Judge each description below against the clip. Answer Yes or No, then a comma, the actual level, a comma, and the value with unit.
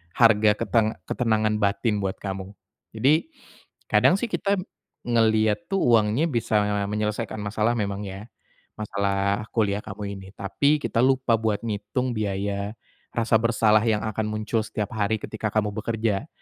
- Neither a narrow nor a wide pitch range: No, narrow, 2.1 semitones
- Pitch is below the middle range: Yes, low, 110 Hz